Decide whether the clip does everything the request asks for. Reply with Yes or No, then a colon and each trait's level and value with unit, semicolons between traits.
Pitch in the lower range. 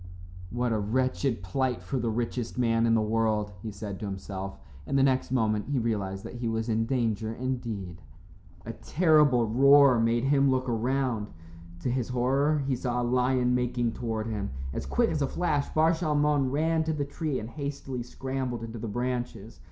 Yes: low, 125 Hz